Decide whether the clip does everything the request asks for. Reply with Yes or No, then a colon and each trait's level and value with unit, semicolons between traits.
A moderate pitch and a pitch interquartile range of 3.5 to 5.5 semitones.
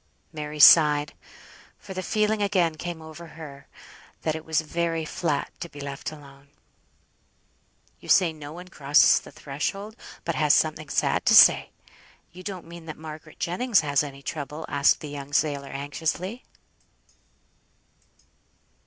No: medium, 155 Hz; average, 2.9 semitones